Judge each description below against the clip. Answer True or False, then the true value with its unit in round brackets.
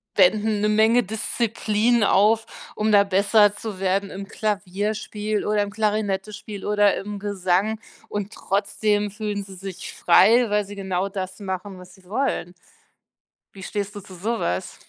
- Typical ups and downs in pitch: False (1.8 semitones)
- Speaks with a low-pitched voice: False (205 Hz)